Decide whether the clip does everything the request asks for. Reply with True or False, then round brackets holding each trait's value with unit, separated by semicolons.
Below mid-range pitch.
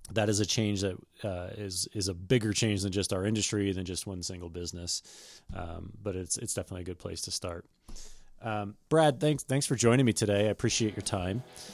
True (100 Hz)